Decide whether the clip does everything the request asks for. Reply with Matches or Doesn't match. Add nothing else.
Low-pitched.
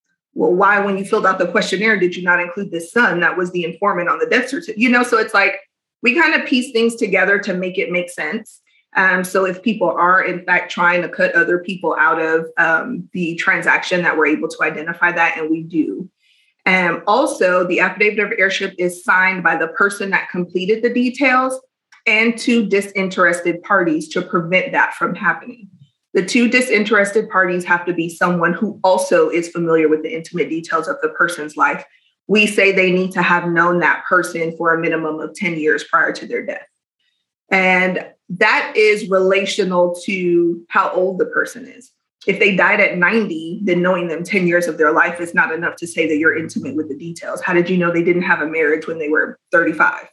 Doesn't match